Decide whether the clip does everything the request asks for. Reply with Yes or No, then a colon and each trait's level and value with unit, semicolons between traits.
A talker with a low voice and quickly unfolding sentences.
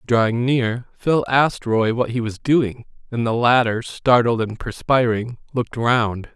No: low, 120 Hz; average, 160 wpm